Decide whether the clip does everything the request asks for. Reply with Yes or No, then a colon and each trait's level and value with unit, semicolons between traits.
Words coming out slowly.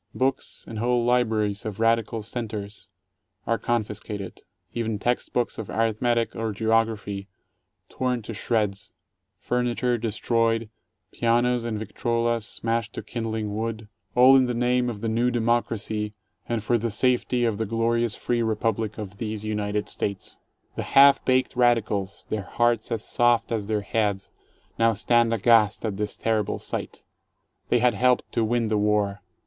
No: average, 155 wpm